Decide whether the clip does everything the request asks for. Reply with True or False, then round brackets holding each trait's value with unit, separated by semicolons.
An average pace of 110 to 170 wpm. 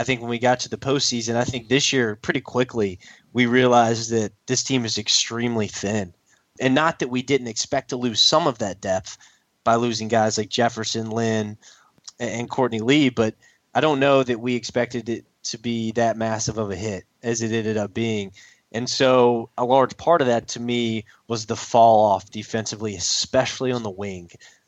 False (195 wpm)